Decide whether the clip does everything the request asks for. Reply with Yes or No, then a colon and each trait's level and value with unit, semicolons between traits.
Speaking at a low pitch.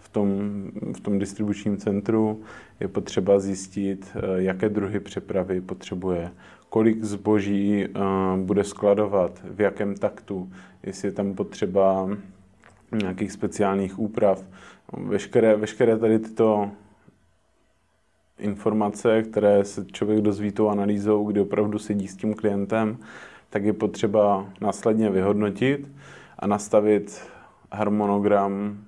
Yes: low, 105 Hz